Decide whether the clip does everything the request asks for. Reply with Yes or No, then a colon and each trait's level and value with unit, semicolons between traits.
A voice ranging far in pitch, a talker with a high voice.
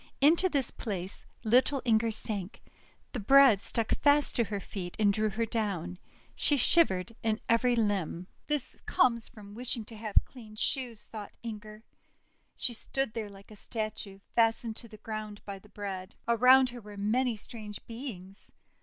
No: average, 3.0 semitones; high, 220 Hz